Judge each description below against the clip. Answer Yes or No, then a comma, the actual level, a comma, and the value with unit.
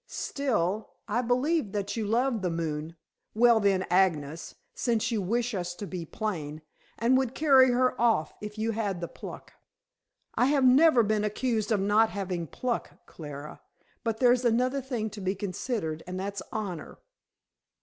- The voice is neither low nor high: No, high, 215 Hz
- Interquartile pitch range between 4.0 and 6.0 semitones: Yes, average, 4.8 semitones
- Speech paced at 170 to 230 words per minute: No, average, 160 wpm